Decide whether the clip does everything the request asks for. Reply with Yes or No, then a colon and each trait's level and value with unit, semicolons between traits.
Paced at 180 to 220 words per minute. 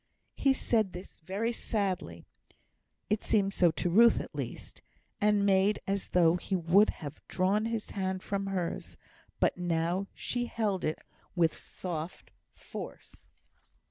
No: average, 140 wpm